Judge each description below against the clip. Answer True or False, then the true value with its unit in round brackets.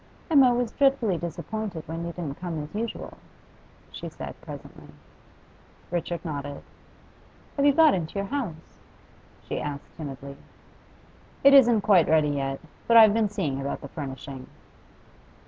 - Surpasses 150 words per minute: False (140 wpm)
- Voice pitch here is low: False (170 Hz)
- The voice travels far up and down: True (7.6 semitones)